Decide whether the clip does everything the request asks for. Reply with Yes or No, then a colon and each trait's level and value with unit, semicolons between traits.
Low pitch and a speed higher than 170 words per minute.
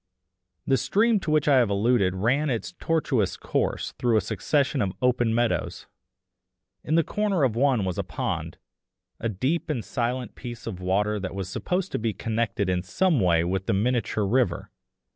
Yes: low, 120 Hz; average, 180 wpm